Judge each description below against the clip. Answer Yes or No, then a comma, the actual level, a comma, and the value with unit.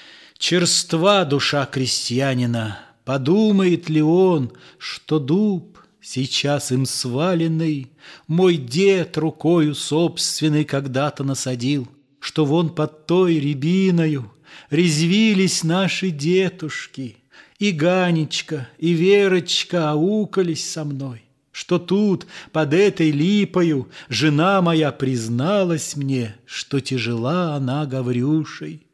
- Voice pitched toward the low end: No, medium, 155 Hz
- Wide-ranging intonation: No, average, 4.5 semitones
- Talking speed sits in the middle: No, slow, 95 wpm